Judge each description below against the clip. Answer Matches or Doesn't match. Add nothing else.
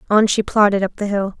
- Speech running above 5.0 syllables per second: Matches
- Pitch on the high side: Matches